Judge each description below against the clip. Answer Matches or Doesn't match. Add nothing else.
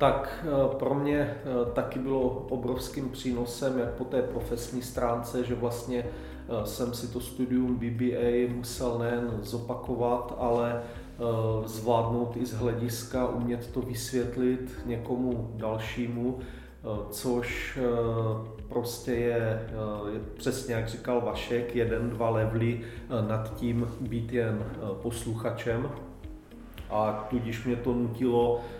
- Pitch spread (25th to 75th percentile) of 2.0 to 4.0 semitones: Doesn't match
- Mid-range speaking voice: Doesn't match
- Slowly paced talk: Matches